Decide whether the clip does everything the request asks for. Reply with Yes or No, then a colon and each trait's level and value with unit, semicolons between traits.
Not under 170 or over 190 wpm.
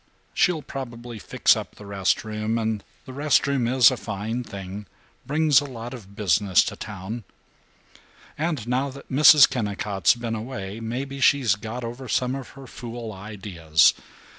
No: average, 160 wpm